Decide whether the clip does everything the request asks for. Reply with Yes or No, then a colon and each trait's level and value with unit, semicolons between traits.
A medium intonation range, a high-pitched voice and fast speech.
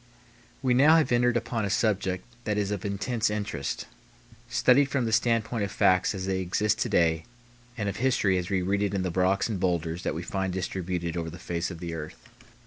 No: average, 3.7 semitones; low, 100 Hz; fast, 215 wpm